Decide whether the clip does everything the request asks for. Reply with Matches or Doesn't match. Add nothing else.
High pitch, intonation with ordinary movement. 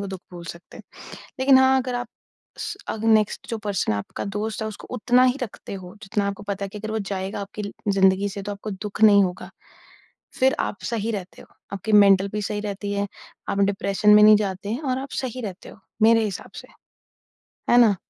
Doesn't match